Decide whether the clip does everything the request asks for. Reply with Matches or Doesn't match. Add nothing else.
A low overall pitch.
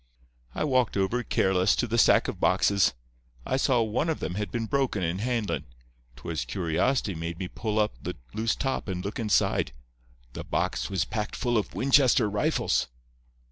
Matches